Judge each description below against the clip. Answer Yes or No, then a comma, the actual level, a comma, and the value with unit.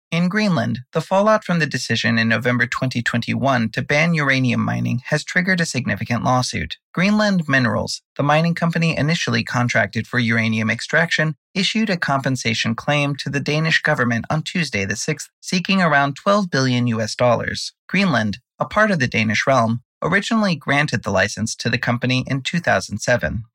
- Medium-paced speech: Yes, average, 160 wpm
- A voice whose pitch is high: No, low, 135 Hz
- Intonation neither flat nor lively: No, wide, 6.0 semitones